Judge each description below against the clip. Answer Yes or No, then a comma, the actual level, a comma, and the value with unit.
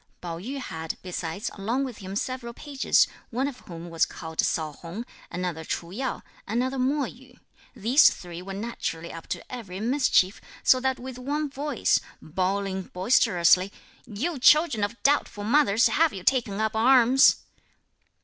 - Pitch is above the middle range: Yes, high, 225 Hz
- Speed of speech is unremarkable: Yes, average, 155 wpm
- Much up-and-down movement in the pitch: Yes, wide, 6.2 semitones